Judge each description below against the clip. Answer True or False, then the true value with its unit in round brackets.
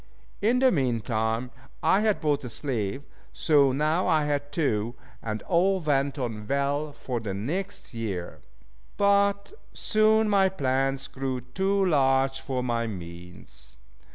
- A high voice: False (135 Hz)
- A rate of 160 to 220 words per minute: False (140 wpm)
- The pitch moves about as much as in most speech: False (6.8 semitones)